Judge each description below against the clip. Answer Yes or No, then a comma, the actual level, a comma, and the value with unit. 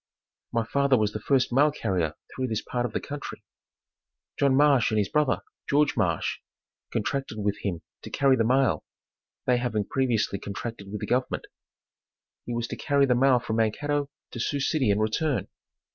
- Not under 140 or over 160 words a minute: No, average, 175 wpm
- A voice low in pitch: Yes, low, 125 Hz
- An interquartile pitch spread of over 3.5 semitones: Yes, average, 4.4 semitones